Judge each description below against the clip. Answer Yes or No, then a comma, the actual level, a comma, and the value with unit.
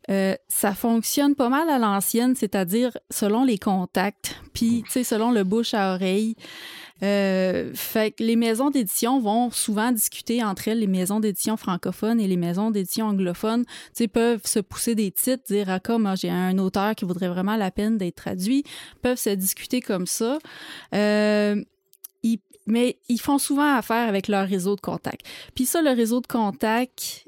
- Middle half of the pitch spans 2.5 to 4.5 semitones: Yes, average, 3.4 semitones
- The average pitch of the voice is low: No, high, 220 Hz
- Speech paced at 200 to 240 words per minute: No, average, 180 wpm